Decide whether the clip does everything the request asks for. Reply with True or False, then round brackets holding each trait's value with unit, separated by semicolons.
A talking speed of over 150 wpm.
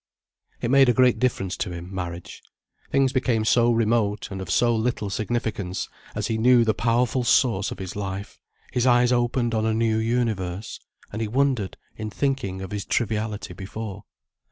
True (175 wpm)